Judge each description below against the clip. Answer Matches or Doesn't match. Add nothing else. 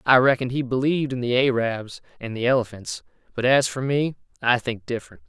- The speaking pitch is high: Doesn't match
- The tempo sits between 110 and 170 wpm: Doesn't match